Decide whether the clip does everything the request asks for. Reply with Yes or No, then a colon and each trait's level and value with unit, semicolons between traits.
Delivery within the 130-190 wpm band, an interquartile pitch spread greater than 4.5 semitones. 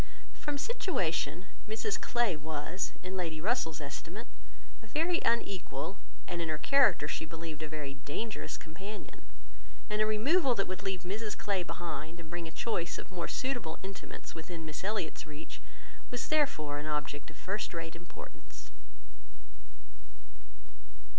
Yes: average, 145 wpm; wide, 5.5 semitones